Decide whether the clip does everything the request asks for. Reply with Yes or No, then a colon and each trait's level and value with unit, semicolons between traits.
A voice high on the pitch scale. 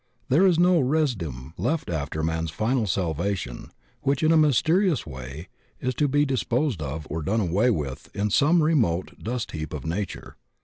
No: low, 105 Hz